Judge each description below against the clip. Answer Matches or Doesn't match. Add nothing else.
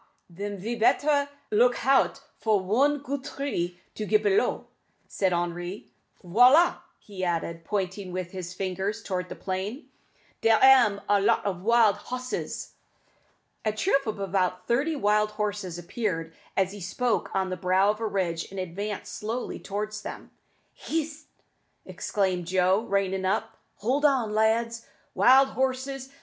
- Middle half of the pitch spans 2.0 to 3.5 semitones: Doesn't match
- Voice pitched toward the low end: Doesn't match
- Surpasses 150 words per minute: Doesn't match